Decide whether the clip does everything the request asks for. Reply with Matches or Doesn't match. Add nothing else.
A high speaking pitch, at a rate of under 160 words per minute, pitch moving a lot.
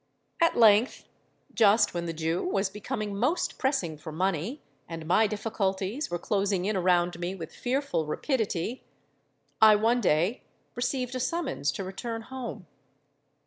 Matches